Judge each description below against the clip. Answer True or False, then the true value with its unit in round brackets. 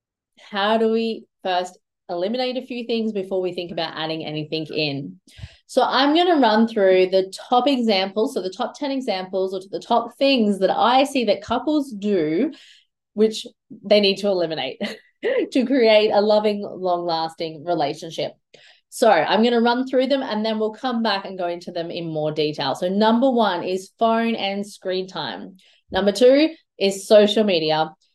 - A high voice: True (205 Hz)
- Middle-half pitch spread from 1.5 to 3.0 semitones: False (4.5 semitones)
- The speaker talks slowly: False (175 wpm)